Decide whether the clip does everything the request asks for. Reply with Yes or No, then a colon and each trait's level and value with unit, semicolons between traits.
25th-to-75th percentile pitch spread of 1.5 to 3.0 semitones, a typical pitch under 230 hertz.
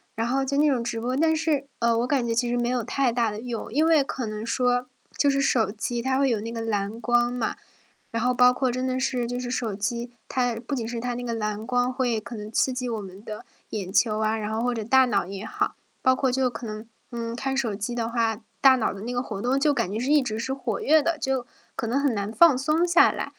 No: narrow, 2.6 semitones; high, 245 Hz